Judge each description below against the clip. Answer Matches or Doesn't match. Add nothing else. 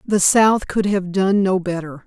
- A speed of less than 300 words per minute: Matches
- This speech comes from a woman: Matches